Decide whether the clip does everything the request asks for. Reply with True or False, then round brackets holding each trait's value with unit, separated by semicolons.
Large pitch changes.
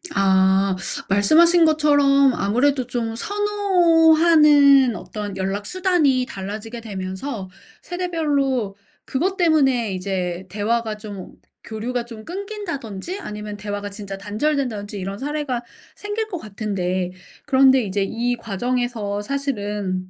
True (6.6 semitones)